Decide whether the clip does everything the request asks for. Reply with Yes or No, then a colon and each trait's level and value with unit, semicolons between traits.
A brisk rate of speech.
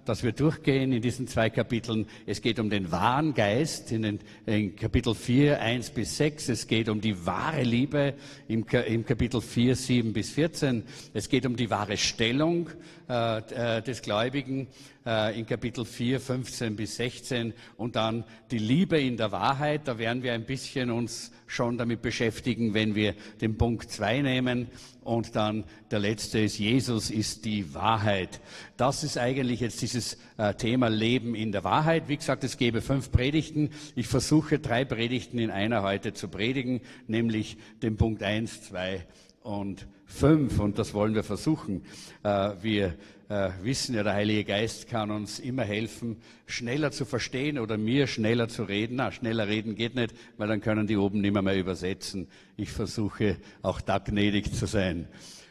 No: average, 170 wpm